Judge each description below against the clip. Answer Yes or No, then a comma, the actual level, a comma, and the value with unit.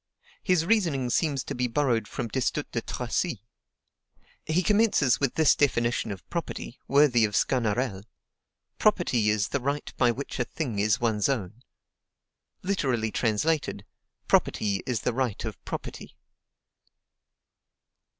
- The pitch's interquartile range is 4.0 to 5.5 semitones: Yes, average, 4.7 semitones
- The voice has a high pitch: No, low, 125 Hz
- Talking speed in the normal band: No, slow, 130 wpm